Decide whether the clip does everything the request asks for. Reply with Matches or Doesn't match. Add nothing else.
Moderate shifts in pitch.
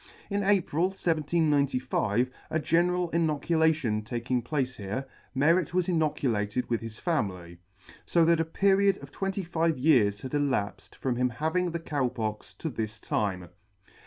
Doesn't match